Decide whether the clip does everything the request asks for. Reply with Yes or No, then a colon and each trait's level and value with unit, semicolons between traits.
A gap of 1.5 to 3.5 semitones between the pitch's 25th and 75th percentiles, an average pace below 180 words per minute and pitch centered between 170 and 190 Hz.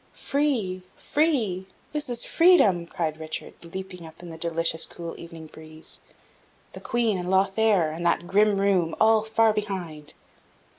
No: average, 4.7 semitones; average, 145 wpm; medium, 185 Hz